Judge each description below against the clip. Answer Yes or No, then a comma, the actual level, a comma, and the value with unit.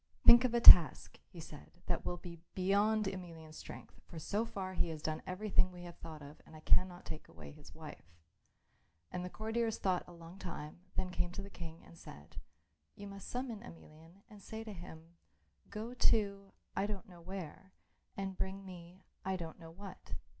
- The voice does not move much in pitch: No, average, 3.2 semitones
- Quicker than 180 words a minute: Yes, average, 195 wpm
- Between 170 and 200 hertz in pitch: Yes, medium, 185 Hz